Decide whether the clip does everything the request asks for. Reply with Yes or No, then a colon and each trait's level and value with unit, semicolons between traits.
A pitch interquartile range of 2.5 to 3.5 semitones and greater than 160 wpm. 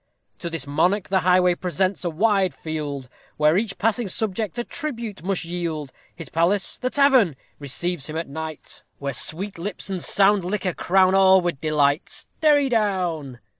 No: average, 4.3 semitones; average, 170 wpm